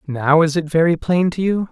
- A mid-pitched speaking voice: Yes, medium, 165 Hz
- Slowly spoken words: No, fast, 245 wpm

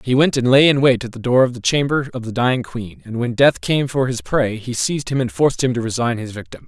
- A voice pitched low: Yes, low, 125 Hz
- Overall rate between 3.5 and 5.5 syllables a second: No, 6.0 syllables/s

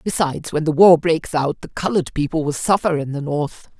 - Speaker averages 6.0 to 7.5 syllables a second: No, 5.5 syllables/s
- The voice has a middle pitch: Yes, medium, 160 Hz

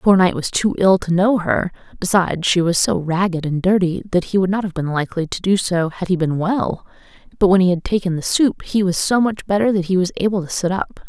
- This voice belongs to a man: No, female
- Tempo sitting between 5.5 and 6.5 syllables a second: Yes, 5.8 syllables/s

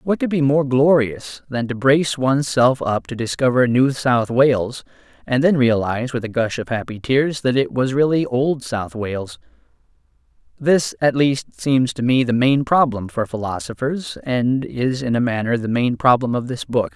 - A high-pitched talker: No, low, 125 Hz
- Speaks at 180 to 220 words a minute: Yes, average, 190 wpm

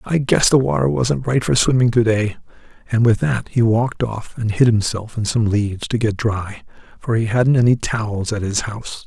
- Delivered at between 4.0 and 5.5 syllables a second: Yes, 5.1 syllables/s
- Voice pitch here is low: Yes, low, 115 Hz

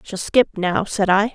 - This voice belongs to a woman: Yes, female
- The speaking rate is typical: No, fast, 225 wpm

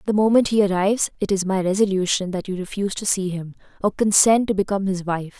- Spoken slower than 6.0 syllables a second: No, 6.4 syllables/s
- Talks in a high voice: Yes, high, 195 Hz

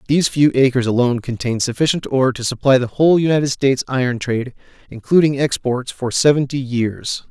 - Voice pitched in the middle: No, low, 130 Hz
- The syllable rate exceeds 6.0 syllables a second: Yes, 6.2 syllables/s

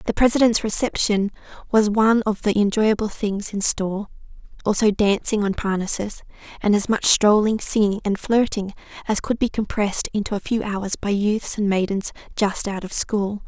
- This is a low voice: No, high, 210 Hz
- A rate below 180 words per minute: Yes, average, 170 wpm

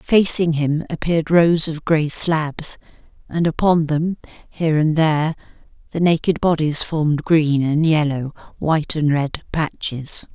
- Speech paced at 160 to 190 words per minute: No, average, 140 wpm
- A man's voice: No, female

